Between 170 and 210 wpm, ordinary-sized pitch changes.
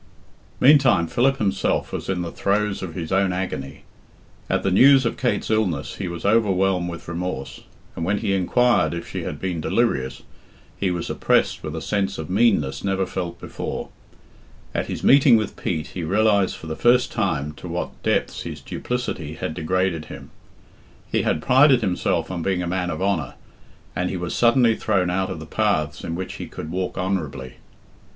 Yes: average, 185 wpm; average, 3.9 semitones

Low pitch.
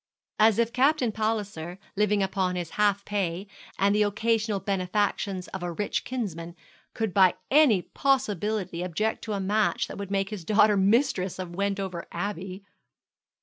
No: high, 200 Hz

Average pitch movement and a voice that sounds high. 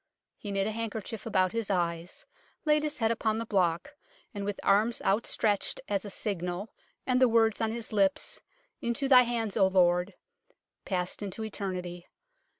Yes: average, 3.4 semitones; high, 205 Hz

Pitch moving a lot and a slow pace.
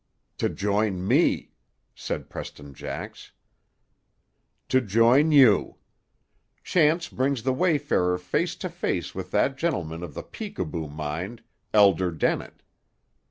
Yes: wide, 7.8 semitones; slow, 115 wpm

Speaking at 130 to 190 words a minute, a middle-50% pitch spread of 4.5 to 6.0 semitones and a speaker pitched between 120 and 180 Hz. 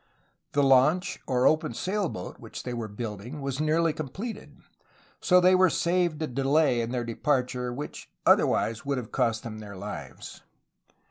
Yes: average, 160 wpm; average, 5.1 semitones; low, 135 Hz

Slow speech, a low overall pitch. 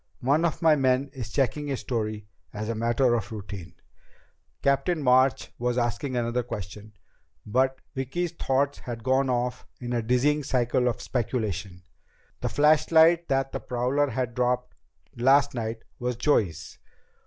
No: average, 145 wpm; low, 125 Hz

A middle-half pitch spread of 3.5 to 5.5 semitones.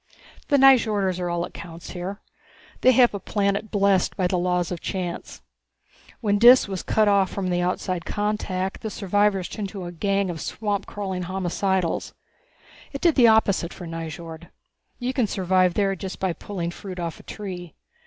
No: narrow, 2.6 semitones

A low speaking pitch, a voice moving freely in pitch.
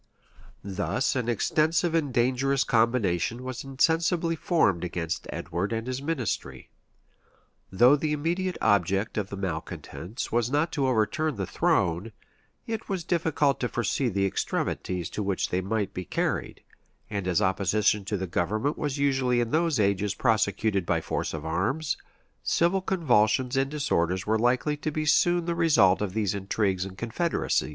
Yes: low, 115 Hz; wide, 7.2 semitones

